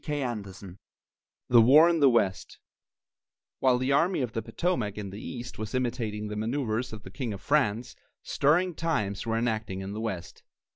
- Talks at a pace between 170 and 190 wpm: Yes, average, 180 wpm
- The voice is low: Yes, low, 115 Hz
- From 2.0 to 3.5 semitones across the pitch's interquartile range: No, average, 4.5 semitones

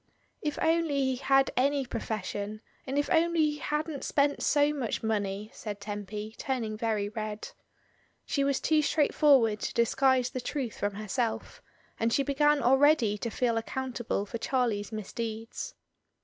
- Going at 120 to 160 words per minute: Yes, average, 150 wpm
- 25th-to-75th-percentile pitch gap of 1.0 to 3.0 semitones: No, average, 4.9 semitones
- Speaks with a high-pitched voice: Yes, very high, 250 Hz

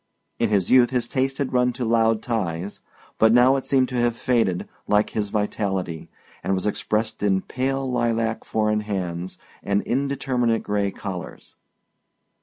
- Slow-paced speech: No, average, 160 wpm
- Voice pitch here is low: Yes, low, 110 Hz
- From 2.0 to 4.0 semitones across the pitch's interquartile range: Yes, average, 3.6 semitones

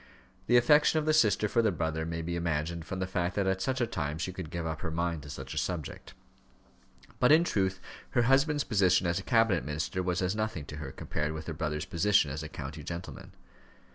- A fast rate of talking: Yes, fast, 230 wpm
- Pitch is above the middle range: No, very low, 90 Hz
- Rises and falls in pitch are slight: No, average, 5.0 semitones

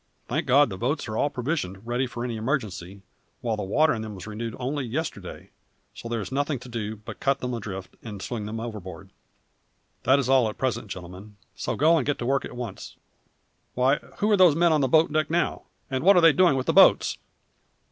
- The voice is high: No, low, 125 Hz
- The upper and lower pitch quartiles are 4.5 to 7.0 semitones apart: Yes, average, 5.1 semitones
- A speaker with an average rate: No, fast, 220 wpm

